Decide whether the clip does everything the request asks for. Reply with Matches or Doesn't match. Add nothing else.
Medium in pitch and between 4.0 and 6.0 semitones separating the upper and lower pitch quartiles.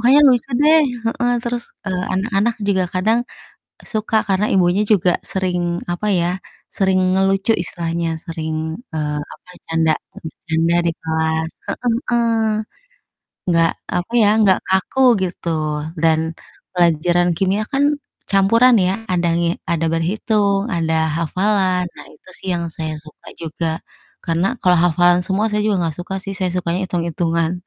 Doesn't match